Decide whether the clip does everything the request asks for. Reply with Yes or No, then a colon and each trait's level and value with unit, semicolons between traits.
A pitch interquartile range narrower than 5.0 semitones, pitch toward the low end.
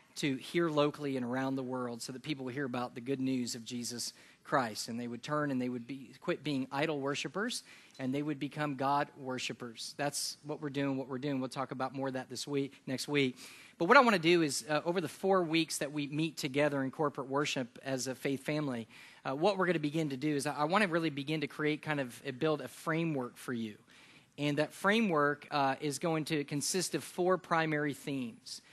No: average, 2.7 semitones; medium, 145 Hz